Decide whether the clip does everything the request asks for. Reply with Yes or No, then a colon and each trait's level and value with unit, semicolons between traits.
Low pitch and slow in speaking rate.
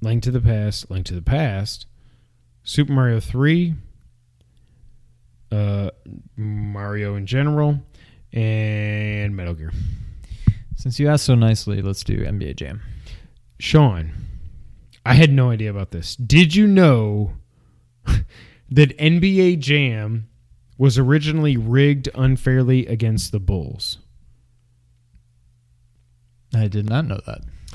Yes: low, 110 Hz; slow, 110 wpm